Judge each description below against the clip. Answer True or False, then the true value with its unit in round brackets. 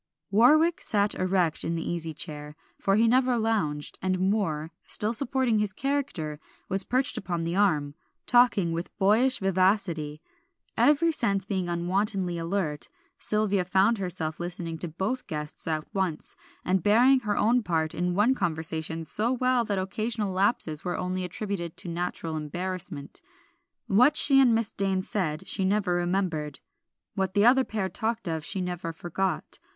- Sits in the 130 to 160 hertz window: False (190 Hz)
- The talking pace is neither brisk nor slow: True (155 wpm)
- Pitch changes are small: False (4.4 semitones)